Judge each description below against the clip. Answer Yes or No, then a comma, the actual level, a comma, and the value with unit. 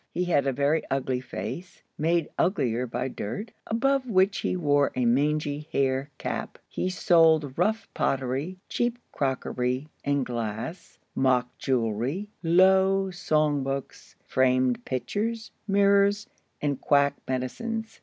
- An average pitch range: No, wide, 6.5 semitones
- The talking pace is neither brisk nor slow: No, slow, 125 wpm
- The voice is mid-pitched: Yes, medium, 145 Hz